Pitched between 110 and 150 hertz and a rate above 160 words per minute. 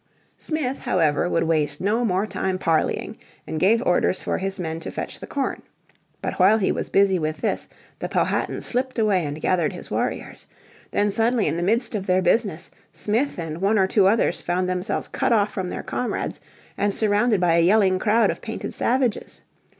No: high, 195 Hz; average, 190 wpm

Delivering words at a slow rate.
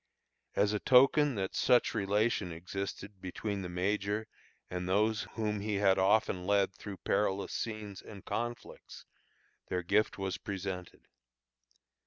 Yes: slow, 130 wpm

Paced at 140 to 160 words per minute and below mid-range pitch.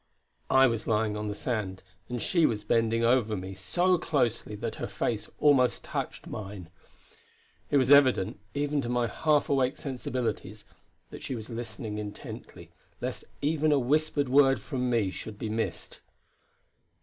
Yes: average, 155 wpm; low, 120 Hz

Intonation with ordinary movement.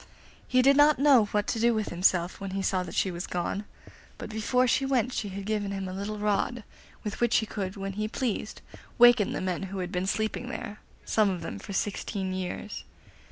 Yes: average, 3.3 semitones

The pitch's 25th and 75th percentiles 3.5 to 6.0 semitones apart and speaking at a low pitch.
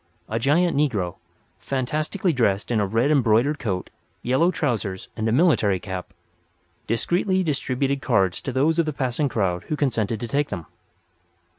Yes: wide, 5.6 semitones; low, 125 Hz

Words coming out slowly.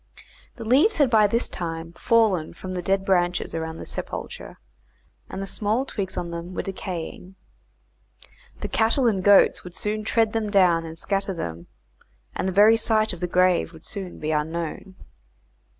No: average, 170 wpm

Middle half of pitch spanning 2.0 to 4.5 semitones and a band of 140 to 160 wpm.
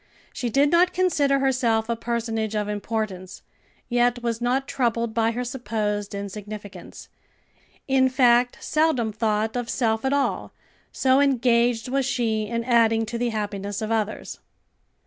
Yes: average, 2.7 semitones; average, 145 wpm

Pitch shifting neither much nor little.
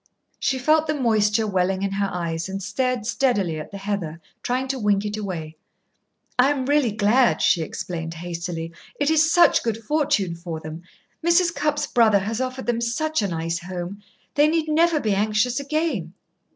No: wide, 7.0 semitones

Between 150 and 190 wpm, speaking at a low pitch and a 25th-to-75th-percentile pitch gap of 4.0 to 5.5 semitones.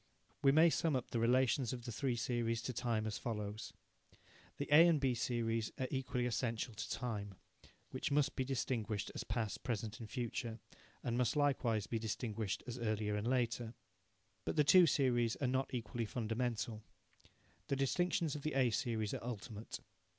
No: average, 170 wpm; low, 120 Hz; average, 2.8 semitones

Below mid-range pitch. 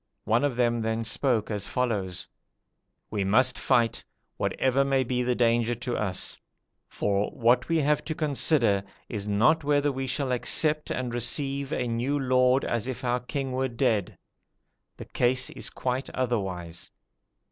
Yes: low, 125 Hz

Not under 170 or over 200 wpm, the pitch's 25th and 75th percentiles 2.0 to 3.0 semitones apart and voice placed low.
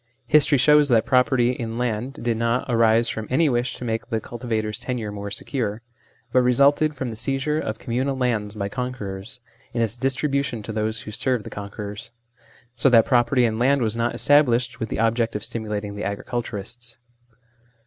Yes: average, 180 wpm; average, 2.7 semitones; low, 120 Hz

